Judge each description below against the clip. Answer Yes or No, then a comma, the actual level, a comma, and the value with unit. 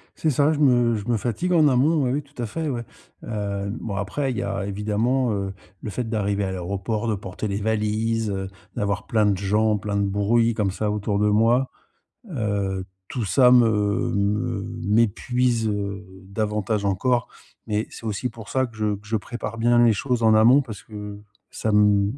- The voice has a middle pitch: No, low, 110 Hz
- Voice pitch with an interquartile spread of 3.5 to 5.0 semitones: No, average, 2.9 semitones